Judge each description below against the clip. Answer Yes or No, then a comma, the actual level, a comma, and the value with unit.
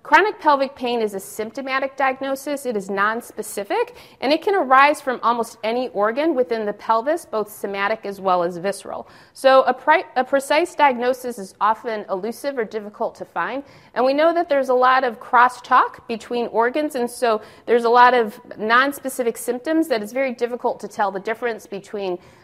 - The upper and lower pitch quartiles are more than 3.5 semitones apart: Yes, average, 3.9 semitones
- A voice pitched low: No, high, 245 Hz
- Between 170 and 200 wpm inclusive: Yes, average, 180 wpm